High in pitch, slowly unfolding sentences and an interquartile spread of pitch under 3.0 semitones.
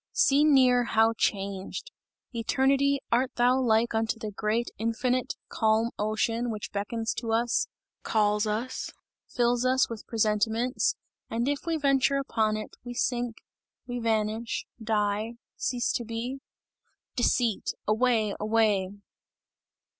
Yes: high, 230 Hz; slow, 125 wpm; narrow, 2.4 semitones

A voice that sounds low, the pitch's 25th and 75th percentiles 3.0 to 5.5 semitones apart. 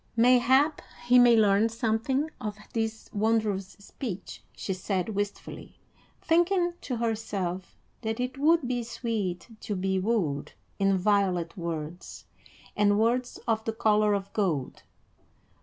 No: high, 220 Hz; average, 3.6 semitones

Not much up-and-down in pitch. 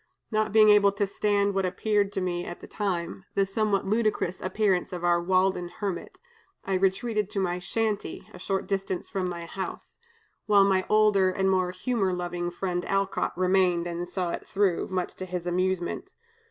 Yes: narrow, 2.1 semitones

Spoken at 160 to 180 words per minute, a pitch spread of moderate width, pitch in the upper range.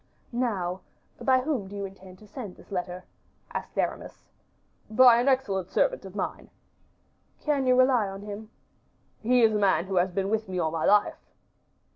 Yes: average, 175 wpm; average, 4.8 semitones; high, 205 Hz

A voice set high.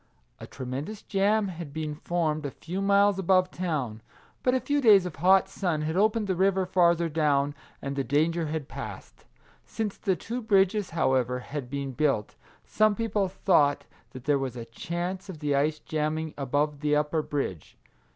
No: medium, 160 Hz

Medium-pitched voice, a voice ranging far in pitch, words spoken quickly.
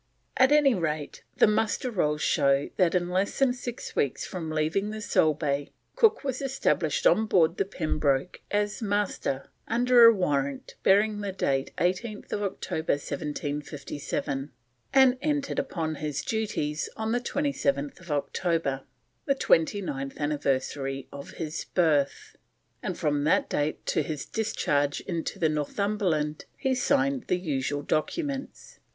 No: medium, 170 Hz; wide, 7.0 semitones; slow, 135 wpm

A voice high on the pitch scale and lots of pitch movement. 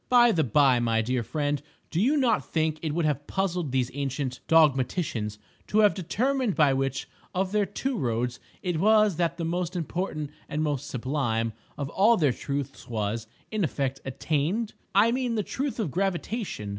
No: medium, 155 Hz; wide, 7.0 semitones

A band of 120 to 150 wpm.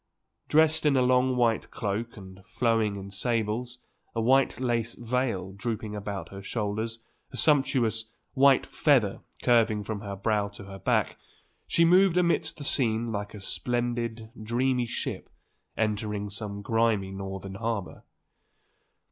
Yes: average, 140 wpm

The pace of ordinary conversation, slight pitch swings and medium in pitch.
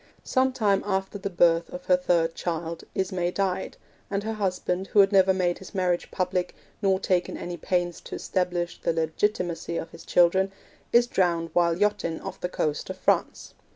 Yes: average, 180 wpm; narrow, 2.1 semitones; medium, 180 Hz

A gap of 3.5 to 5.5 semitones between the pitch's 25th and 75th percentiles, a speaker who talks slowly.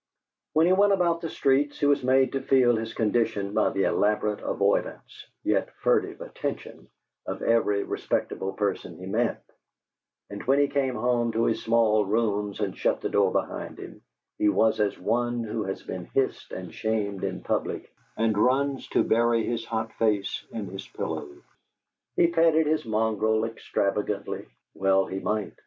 No: average, 4.1 semitones; average, 165 wpm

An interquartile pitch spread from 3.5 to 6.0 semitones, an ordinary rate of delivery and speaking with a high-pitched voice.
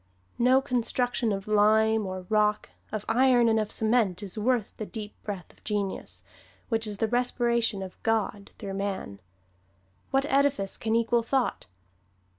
No: average, 2.7 semitones; average, 150 wpm; high, 220 Hz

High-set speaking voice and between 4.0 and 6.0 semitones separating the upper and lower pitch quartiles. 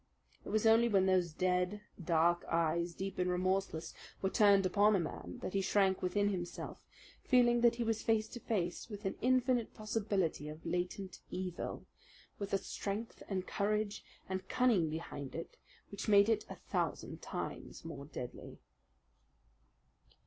No: high, 195 Hz; average, 3.3 semitones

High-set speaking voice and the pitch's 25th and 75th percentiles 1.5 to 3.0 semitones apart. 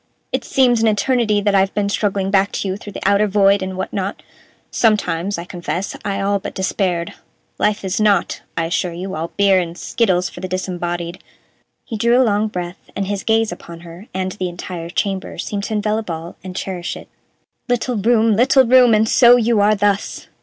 Yes: high, 200 Hz; average, 2.7 semitones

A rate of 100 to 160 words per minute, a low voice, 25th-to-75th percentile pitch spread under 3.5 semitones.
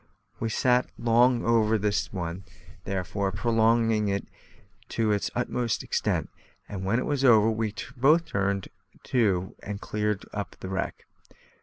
Yes: average, 140 wpm; low, 110 Hz; average, 2.9 semitones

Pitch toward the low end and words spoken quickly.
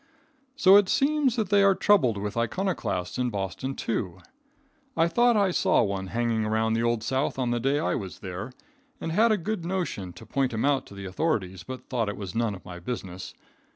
Yes: low, 120 Hz; fast, 210 wpm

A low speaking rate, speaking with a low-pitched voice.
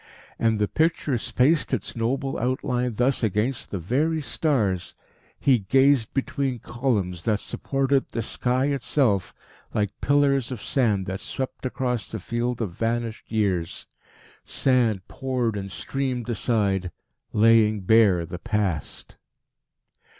Yes: slow, 125 wpm; low, 115 Hz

